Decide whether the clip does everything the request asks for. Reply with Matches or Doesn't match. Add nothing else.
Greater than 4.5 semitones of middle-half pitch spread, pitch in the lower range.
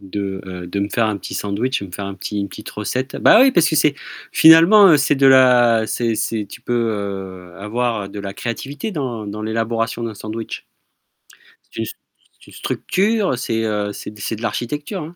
Matches